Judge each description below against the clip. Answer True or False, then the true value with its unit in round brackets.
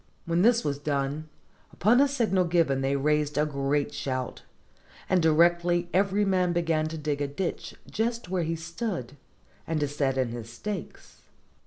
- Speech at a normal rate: True (165 wpm)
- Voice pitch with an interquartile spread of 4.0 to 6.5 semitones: True (4.3 semitones)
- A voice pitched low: False (160 Hz)